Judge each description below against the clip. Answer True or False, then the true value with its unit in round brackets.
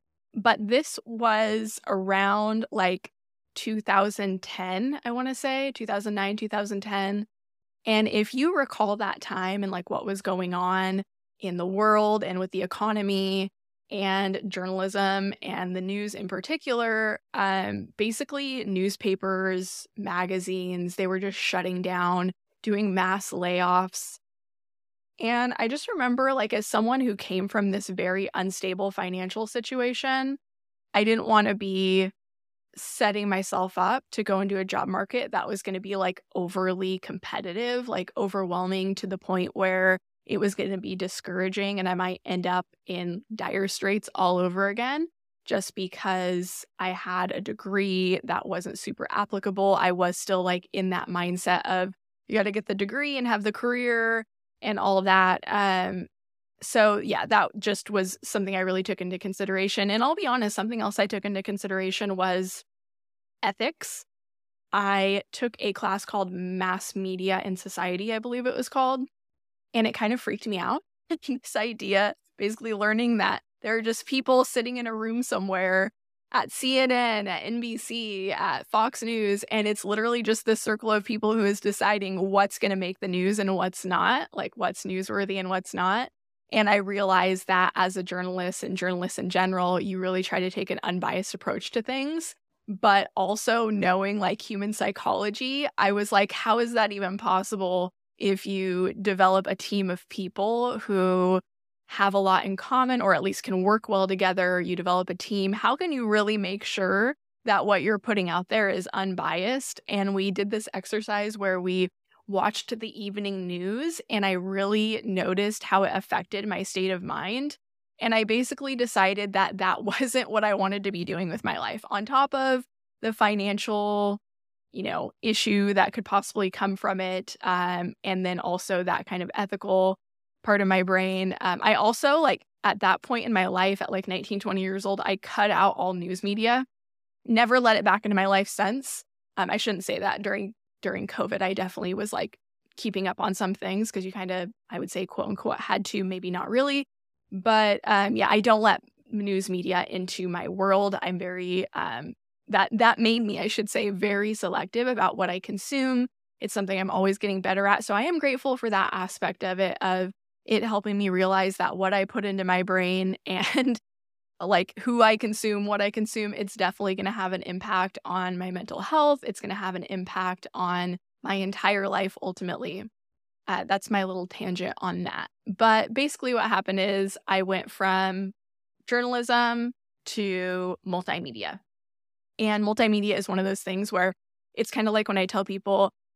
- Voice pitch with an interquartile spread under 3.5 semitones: True (2.6 semitones)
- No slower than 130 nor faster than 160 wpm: False (180 wpm)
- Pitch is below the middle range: False (195 Hz)